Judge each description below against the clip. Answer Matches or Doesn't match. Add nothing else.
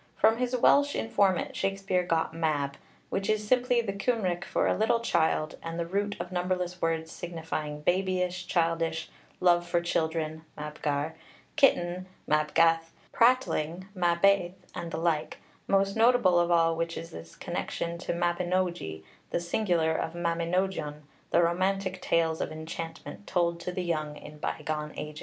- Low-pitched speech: Doesn't match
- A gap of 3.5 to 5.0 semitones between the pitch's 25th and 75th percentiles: Doesn't match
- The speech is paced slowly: Doesn't match